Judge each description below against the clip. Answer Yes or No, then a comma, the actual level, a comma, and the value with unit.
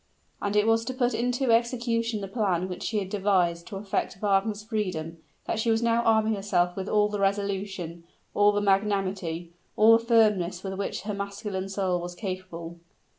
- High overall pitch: Yes, high, 200 Hz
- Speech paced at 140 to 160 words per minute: No, average, 180 wpm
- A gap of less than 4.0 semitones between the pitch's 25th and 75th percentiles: Yes, average, 2.9 semitones